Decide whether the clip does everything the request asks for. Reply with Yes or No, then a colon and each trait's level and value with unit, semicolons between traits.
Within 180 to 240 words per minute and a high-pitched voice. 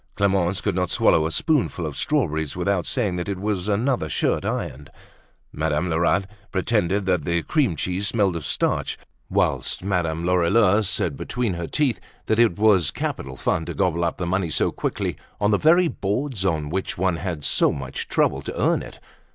No: average, 185 wpm; very low, 90 Hz